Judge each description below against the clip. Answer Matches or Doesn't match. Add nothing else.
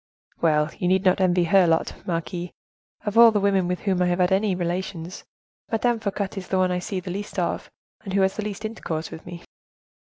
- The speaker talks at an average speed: Doesn't match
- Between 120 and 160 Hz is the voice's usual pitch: Doesn't match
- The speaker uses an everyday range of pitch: Doesn't match